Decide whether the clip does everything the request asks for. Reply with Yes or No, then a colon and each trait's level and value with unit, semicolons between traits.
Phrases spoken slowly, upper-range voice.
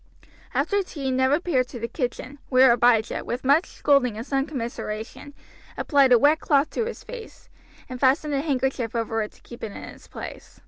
No: average, 190 wpm; very high, 265 Hz